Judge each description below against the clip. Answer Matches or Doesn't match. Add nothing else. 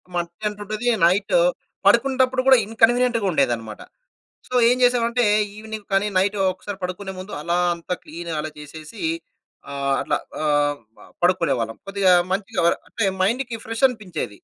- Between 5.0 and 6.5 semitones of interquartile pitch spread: Matches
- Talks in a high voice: Matches